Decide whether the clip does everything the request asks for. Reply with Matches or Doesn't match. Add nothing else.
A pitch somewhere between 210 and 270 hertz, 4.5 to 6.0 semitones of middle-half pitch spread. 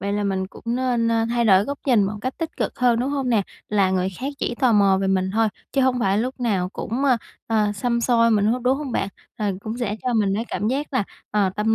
Doesn't match